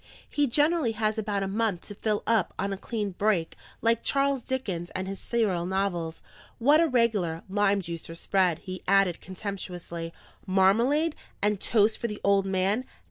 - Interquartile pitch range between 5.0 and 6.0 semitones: No, average, 3.6 semitones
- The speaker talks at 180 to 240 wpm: No, average, 165 wpm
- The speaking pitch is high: Yes, high, 200 Hz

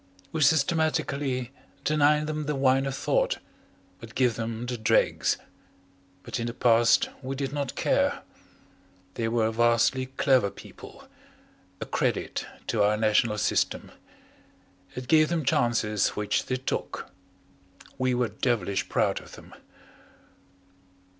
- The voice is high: No, low, 125 Hz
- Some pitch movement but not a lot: Yes, average, 3.8 semitones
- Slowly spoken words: Yes, slow, 125 wpm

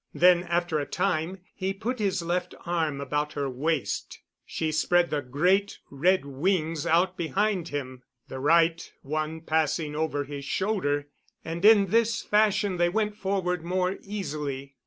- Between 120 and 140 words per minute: No, average, 150 wpm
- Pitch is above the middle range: No, medium, 170 Hz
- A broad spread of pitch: No, average, 4.3 semitones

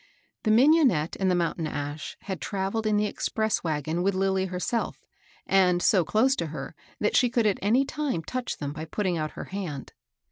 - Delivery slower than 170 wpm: No, average, 190 wpm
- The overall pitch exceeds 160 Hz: Yes, high, 190 Hz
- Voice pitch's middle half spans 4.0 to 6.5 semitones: Yes, average, 5.0 semitones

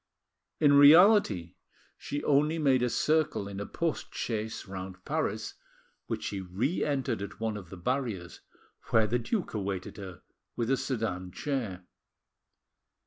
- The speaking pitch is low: Yes, low, 115 Hz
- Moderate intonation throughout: No, wide, 6.8 semitones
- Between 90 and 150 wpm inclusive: Yes, average, 140 wpm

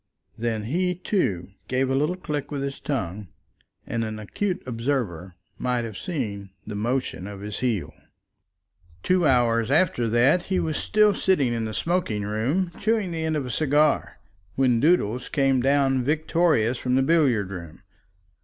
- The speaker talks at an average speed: Yes, average, 160 wpm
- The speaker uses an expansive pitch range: Yes, wide, 6.1 semitones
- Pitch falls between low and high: No, low, 130 Hz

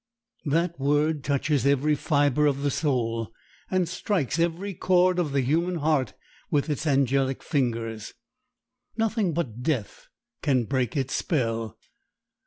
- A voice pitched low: No, medium, 145 Hz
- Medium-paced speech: No, slow, 130 wpm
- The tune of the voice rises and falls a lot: No, average, 4.1 semitones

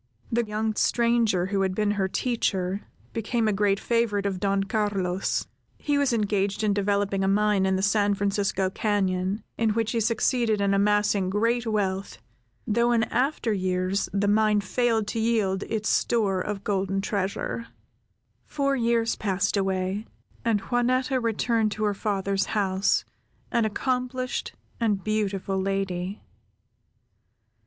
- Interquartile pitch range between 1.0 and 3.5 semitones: Yes, average, 2.7 semitones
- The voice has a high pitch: Yes, high, 205 Hz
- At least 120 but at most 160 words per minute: Yes, average, 140 wpm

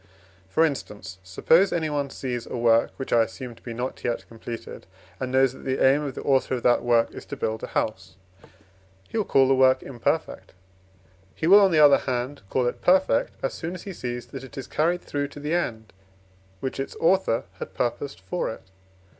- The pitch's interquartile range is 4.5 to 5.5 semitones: No, average, 3.8 semitones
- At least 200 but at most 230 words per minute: Yes, fast, 205 wpm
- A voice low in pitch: Yes, low, 130 Hz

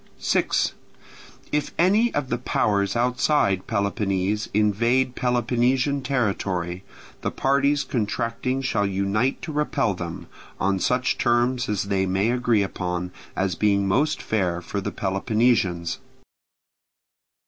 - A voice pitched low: Yes, low, 110 Hz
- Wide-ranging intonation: No, average, 4.7 semitones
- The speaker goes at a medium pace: No, slow, 115 wpm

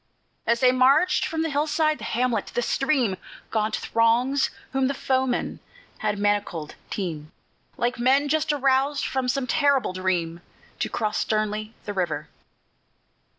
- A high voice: Yes, very high, 250 Hz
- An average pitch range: Yes, average, 4.7 semitones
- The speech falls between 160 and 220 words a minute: No, average, 140 wpm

